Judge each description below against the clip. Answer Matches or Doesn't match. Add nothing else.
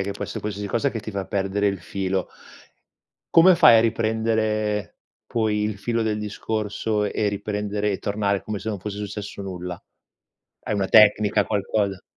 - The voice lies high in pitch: Doesn't match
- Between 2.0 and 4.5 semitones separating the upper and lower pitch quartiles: Doesn't match